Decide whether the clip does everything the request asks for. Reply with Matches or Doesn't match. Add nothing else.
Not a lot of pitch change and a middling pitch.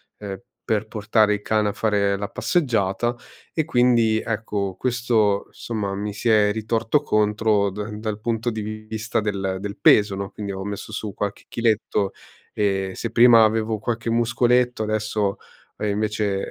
Doesn't match